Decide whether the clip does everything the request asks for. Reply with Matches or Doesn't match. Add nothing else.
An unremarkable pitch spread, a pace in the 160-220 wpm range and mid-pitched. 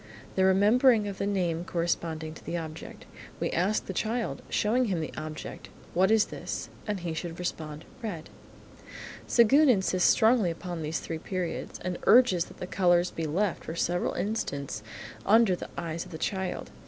Matches